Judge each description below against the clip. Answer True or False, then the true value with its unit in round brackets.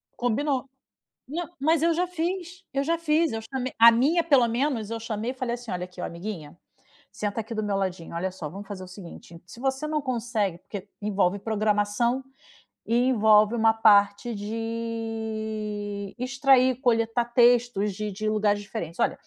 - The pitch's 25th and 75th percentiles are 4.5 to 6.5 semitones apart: False (3.8 semitones)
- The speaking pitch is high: True (225 Hz)